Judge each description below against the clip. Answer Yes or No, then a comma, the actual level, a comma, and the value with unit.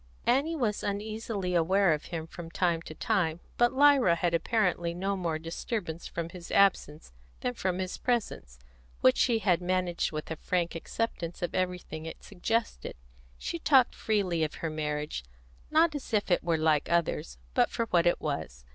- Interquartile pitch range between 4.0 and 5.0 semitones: Yes, average, 4.7 semitones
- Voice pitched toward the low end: No, medium, 175 Hz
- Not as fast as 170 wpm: No, average, 175 wpm